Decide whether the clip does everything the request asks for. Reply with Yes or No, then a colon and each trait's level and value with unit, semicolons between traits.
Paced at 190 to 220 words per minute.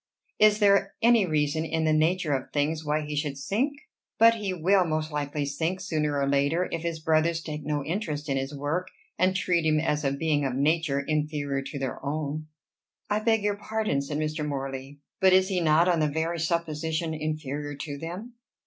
Yes: average, 195 wpm